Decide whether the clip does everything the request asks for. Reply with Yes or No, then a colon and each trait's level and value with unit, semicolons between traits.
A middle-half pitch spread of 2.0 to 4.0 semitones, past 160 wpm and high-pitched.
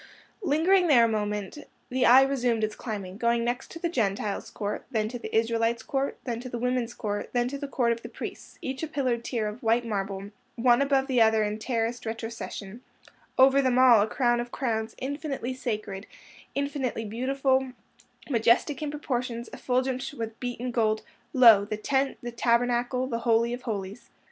Yes: average, 2.8 semitones; average, 180 wpm; high, 240 Hz